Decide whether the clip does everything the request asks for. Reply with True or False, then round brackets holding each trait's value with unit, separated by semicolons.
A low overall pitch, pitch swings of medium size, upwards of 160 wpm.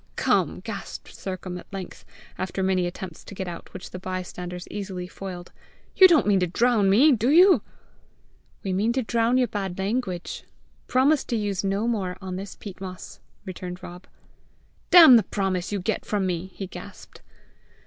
False (195 Hz; 3.6 semitones; 170 wpm)